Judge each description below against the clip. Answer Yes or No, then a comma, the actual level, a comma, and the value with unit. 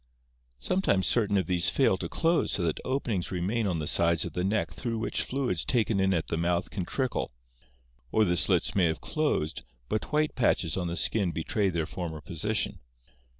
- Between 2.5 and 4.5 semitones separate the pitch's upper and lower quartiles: No, average, 5.0 semitones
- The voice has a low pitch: Yes, very low, 95 Hz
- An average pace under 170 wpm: No, average, 195 wpm